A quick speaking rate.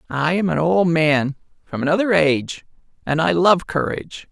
No: average, 165 wpm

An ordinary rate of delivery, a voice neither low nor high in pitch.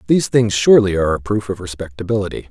No: average, 190 wpm; low, 105 Hz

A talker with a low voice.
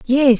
No: very high, 255 Hz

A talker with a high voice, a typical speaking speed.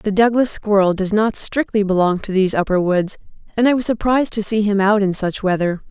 No: high, 205 Hz; fast, 225 wpm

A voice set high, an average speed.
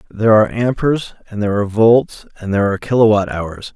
No: low, 105 Hz; average, 190 wpm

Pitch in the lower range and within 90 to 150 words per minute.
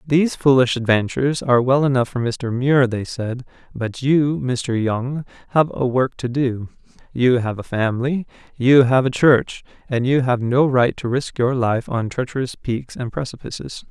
No: low, 125 Hz; average, 180 wpm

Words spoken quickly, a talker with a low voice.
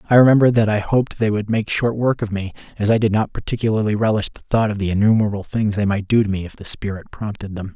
Yes: fast, 265 wpm; low, 105 Hz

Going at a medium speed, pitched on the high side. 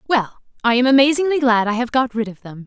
No: fast, 245 wpm; high, 240 Hz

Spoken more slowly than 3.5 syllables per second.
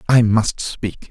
Yes: 3.2 syllables/s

